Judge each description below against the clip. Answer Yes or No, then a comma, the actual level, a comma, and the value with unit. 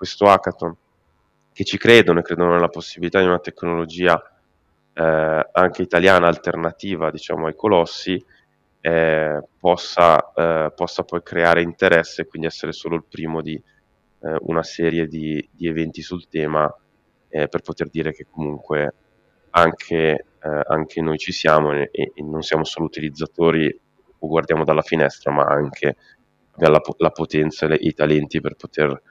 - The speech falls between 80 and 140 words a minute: No, average, 155 wpm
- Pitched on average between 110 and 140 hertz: No, very low, 80 Hz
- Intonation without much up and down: Yes, narrow, 1.8 semitones